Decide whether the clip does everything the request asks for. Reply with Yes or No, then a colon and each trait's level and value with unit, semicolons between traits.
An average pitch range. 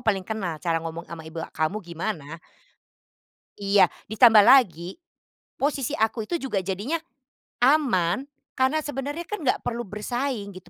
No: wide, 7.2 semitones